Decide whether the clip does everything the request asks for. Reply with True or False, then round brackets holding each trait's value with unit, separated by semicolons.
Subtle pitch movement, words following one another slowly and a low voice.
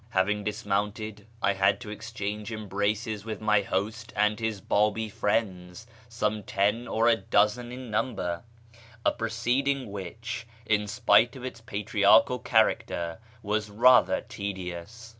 True (1.9 semitones; 130 wpm; 105 Hz)